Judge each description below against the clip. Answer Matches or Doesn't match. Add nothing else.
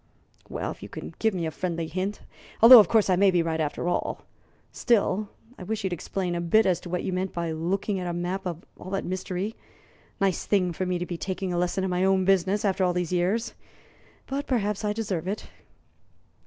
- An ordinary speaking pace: Doesn't match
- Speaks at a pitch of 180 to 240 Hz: Matches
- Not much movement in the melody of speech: Matches